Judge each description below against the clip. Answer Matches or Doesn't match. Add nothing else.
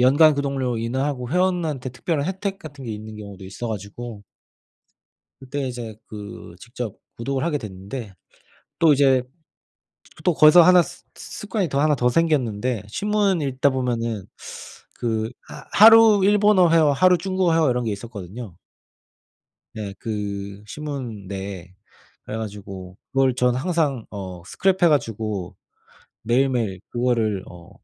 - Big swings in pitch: Matches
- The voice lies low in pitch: Matches